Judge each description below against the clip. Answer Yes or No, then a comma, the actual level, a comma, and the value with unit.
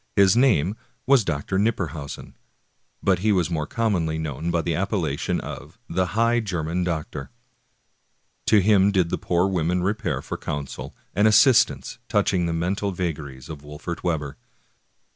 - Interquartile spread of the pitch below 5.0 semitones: Yes, average, 4.2 semitones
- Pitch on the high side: No, very low, 90 Hz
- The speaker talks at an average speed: Yes, average, 160 wpm